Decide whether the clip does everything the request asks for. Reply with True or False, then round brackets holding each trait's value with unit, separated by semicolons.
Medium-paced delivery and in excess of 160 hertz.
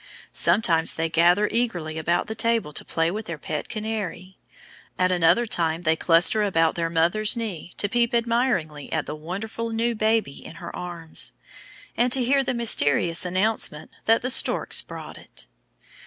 True (165 wpm; 185 Hz)